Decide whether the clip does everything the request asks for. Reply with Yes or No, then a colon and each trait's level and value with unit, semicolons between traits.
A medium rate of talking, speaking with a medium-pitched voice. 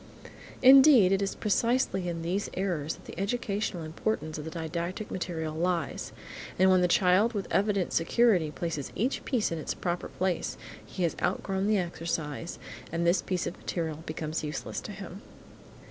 Yes: average, 165 wpm; medium, 180 Hz